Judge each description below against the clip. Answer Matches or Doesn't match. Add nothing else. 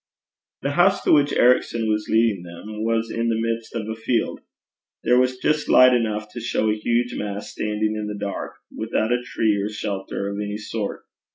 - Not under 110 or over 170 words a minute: Doesn't match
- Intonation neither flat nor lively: Doesn't match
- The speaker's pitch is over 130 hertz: Doesn't match